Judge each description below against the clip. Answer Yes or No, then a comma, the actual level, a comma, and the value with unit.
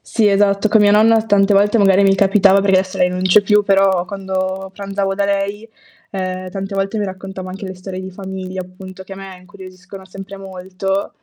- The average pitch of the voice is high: Yes, high, 195 Hz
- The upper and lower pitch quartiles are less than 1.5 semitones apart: Yes, narrow, 1.1 semitones